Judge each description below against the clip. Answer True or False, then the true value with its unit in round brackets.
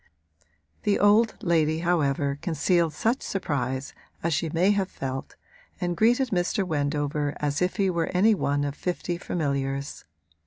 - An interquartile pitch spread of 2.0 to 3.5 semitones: False (4.5 semitones)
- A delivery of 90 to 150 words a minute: True (145 wpm)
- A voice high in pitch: False (165 Hz)